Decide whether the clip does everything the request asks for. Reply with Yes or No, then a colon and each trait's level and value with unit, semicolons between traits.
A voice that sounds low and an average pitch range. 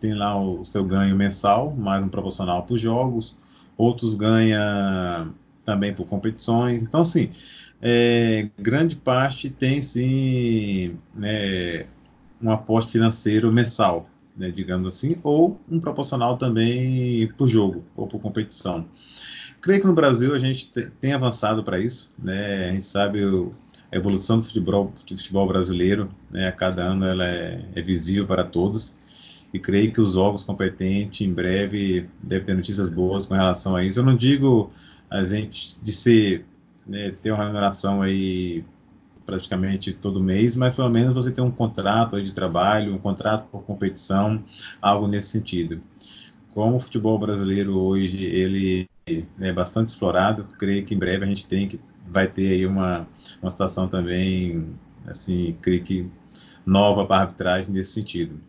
Yes: low, 100 Hz; average, 3.4 semitones